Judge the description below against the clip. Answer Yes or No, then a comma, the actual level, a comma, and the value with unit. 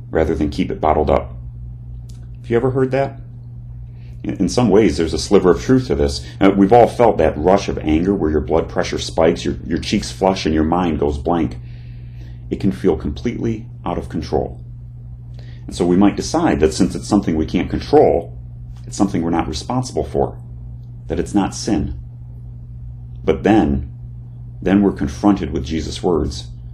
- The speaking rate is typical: Yes, average, 180 wpm